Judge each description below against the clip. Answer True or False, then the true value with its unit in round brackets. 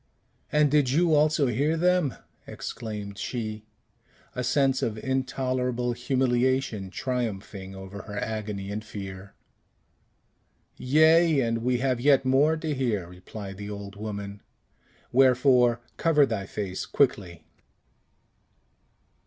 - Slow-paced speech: True (110 wpm)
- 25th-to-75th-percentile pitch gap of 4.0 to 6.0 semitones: True (4.8 semitones)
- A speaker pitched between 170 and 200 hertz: False (120 Hz)